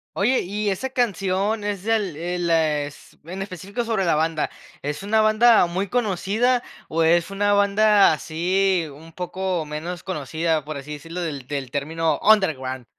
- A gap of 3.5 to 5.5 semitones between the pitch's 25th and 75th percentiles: Yes, average, 4.4 semitones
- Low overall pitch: No, medium, 180 Hz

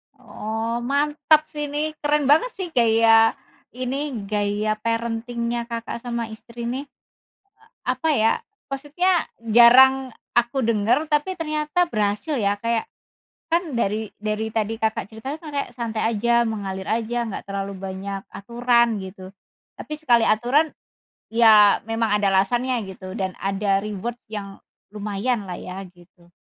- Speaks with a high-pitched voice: Yes, high, 230 Hz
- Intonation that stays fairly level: No, average, 3.8 semitones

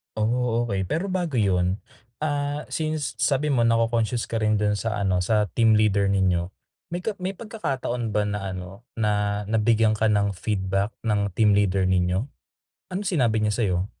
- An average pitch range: Yes, average, 3.6 semitones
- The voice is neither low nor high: No, low, 110 Hz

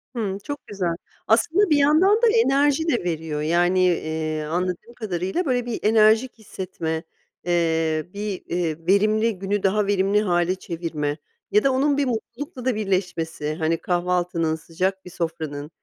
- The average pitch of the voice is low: No, high, 190 Hz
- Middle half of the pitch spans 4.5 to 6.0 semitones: Yes, wide, 5.6 semitones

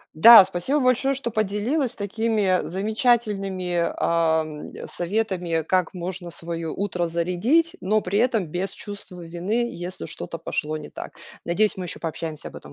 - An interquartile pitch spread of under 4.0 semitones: No, average, 4.3 semitones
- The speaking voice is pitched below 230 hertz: Yes, medium, 185 Hz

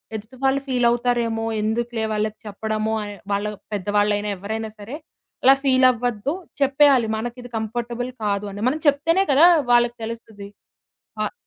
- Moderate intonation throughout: Yes, average, 3.1 semitones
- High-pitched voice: Yes, high, 230 Hz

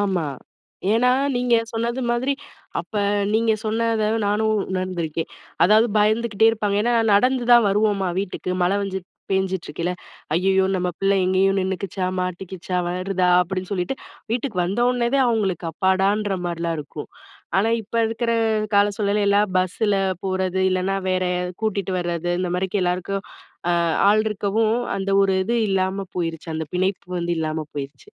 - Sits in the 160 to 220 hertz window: Yes, high, 195 Hz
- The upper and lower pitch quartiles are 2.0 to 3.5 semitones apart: Yes, average, 2.8 semitones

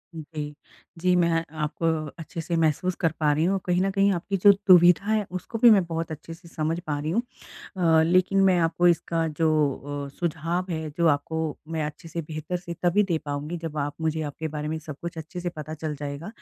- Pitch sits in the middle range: Yes, medium, 165 Hz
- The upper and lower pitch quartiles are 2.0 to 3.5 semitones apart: Yes, narrow, 2.4 semitones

